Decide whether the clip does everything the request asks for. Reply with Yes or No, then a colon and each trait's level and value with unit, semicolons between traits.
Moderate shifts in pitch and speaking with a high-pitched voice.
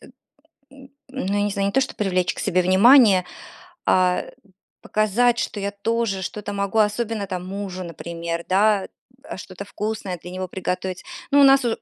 Yes: average, 3.4 semitones; high, 200 Hz